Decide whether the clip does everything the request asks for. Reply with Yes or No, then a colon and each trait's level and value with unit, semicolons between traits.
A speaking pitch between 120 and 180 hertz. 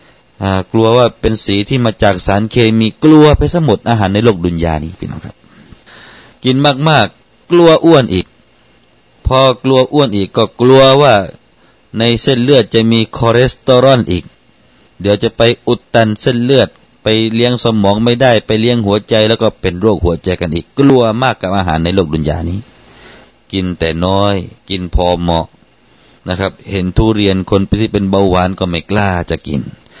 No: low, 110 Hz